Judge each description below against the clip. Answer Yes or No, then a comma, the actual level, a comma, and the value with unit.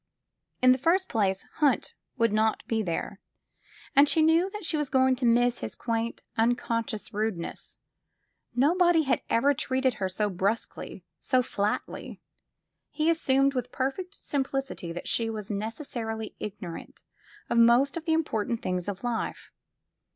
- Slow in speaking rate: No, average, 145 wpm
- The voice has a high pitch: Yes, high, 245 Hz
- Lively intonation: No, average, 4.4 semitones